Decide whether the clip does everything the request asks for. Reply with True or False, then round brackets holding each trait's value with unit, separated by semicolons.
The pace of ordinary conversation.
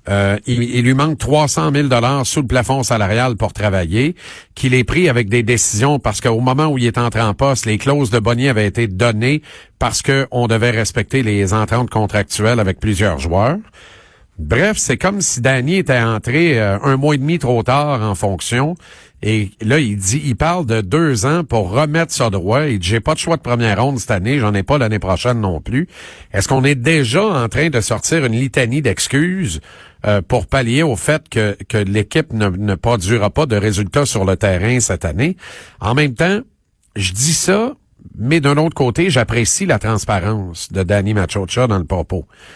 True (200 wpm)